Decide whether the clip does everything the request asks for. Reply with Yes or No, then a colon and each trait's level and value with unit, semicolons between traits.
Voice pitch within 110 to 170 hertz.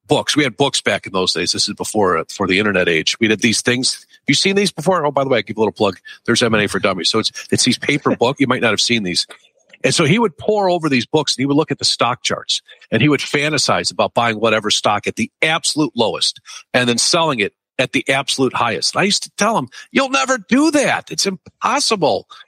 Yes: medium, 140 Hz